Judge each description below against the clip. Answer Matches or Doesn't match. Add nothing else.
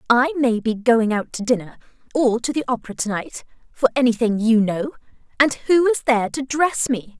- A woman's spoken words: Matches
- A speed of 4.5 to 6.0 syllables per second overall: Matches